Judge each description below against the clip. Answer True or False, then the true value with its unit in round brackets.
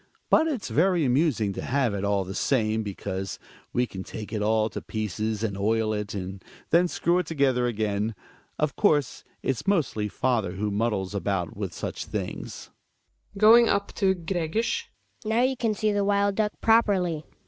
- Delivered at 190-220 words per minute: False (175 wpm)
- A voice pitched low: True (125 Hz)